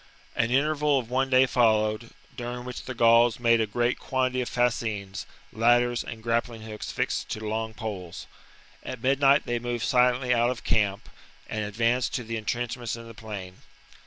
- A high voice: No, low, 120 Hz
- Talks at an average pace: Yes, average, 170 wpm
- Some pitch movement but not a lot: No, narrow, 2.0 semitones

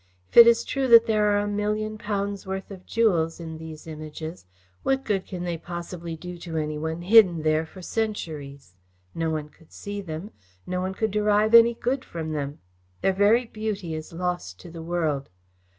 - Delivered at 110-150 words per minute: No, average, 190 wpm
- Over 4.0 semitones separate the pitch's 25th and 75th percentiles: Yes, average, 4.7 semitones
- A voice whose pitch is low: No, medium, 180 Hz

